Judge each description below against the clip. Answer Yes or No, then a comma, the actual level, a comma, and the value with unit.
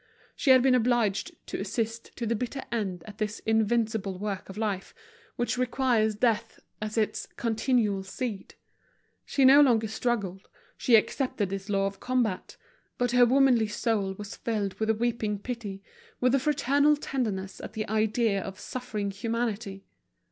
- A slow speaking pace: No, average, 155 wpm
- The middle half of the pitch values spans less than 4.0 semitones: Yes, average, 3.3 semitones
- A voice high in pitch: Yes, high, 220 Hz